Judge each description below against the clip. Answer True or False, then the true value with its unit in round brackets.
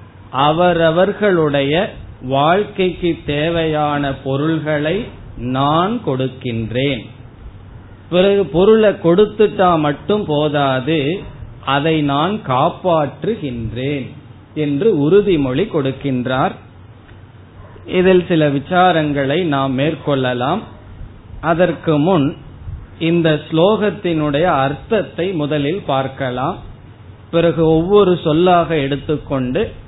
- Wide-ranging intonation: False (4.9 semitones)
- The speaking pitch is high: False (145 Hz)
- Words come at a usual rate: False (65 wpm)